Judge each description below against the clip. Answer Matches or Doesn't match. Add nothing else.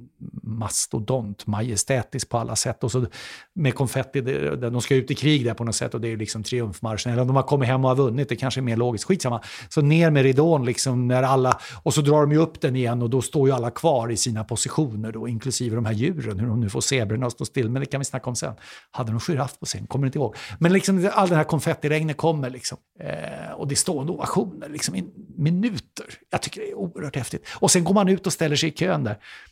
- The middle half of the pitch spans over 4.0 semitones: Matches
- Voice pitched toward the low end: Matches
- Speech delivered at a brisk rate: Matches